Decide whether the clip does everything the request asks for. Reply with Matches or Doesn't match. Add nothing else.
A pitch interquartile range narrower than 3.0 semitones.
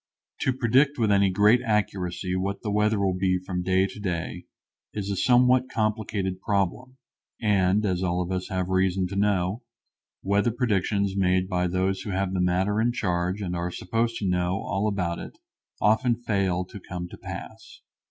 Matches